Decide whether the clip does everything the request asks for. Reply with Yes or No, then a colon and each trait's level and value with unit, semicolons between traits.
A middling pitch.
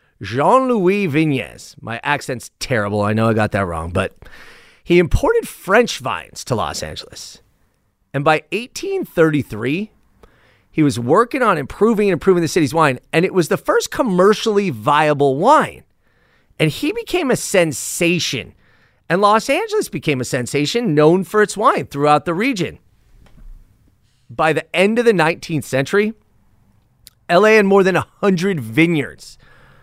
Yes: medium, 155 Hz